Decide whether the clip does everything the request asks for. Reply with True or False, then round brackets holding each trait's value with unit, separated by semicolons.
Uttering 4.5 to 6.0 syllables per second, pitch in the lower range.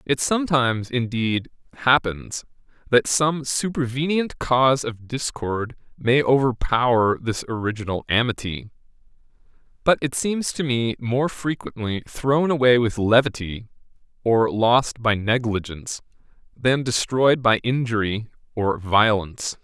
False (4.2 syllables/s; 120 Hz)